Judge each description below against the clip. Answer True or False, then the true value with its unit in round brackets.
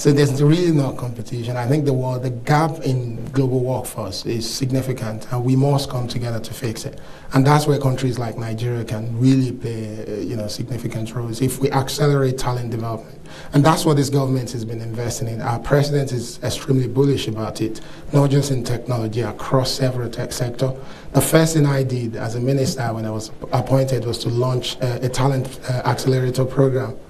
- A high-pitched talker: False (130 Hz)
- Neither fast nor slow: True (195 wpm)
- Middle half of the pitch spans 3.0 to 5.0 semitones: False (2.5 semitones)